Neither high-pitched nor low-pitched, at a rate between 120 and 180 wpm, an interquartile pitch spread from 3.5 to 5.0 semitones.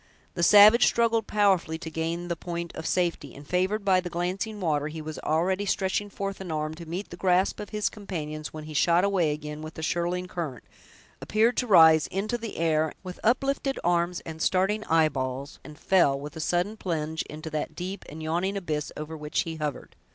No: medium, 170 Hz; average, 200 wpm; average, 3.8 semitones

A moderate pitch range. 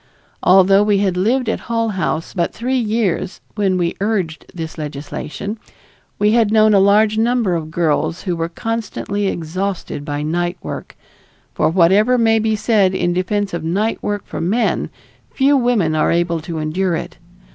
Yes: average, 4.3 semitones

